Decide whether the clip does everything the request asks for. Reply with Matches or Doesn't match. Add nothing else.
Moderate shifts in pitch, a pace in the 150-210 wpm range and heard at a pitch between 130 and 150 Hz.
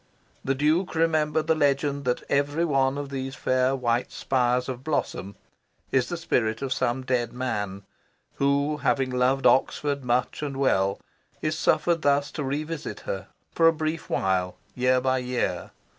Matches